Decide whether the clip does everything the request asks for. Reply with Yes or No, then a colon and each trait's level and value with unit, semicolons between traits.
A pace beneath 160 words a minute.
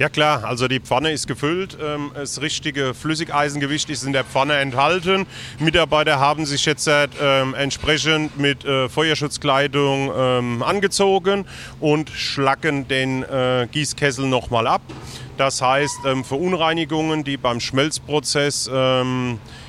Yes: average, 130 wpm